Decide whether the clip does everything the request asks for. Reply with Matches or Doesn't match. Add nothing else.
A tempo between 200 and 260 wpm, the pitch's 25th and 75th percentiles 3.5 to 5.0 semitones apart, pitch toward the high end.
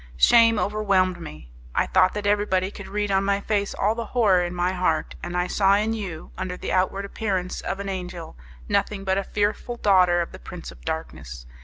Doesn't match